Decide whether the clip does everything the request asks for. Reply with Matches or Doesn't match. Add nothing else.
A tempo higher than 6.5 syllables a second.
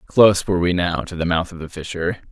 Matches